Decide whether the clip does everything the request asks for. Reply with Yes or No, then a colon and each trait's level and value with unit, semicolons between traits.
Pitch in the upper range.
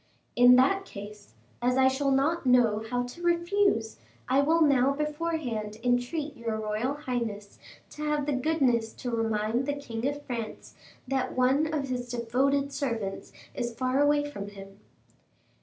Yes: very high, 255 Hz